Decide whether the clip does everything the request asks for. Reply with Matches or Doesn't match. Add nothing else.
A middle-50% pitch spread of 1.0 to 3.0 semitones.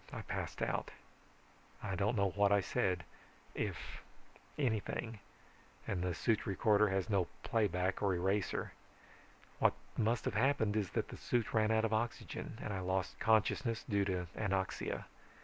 Matches